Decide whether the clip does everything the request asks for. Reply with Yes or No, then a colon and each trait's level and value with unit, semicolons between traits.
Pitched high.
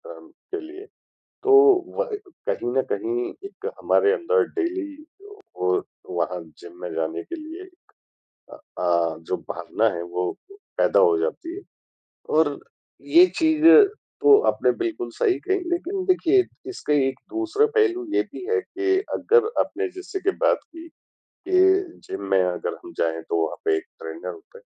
Yes: very high, 360 Hz